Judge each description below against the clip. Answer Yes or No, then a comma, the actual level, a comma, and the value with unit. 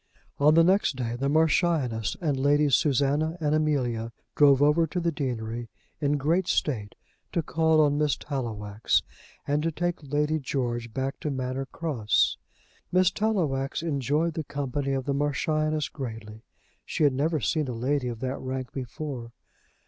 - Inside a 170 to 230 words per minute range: No, average, 155 wpm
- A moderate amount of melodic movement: Yes, average, 3.3 semitones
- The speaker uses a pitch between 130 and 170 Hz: Yes, medium, 140 Hz